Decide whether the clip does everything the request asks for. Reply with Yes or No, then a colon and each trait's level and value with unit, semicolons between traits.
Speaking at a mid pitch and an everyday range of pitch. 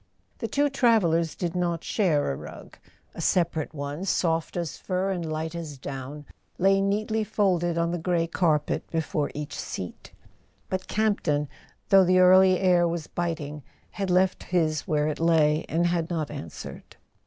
Yes: medium, 170 Hz; average, 3.1 semitones